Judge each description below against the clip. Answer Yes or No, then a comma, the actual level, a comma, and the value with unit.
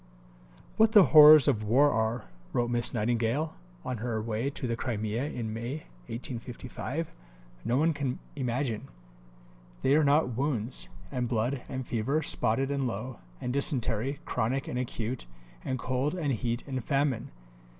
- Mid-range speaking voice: No, low, 125 Hz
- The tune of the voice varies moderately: Yes, average, 3.3 semitones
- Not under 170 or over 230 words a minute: No, average, 150 wpm